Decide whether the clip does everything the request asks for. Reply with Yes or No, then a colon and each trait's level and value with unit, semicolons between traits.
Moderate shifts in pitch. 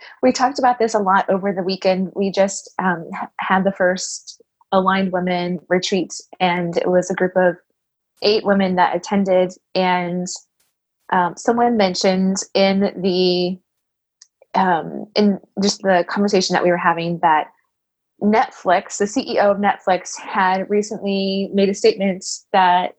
No: narrow, 1.8 semitones